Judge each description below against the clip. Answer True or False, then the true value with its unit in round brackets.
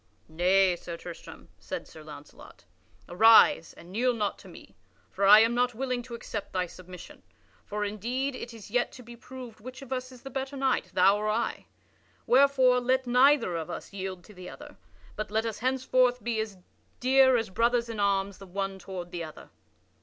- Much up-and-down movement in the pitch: False (4.6 semitones)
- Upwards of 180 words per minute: True (190 wpm)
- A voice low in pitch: False (225 Hz)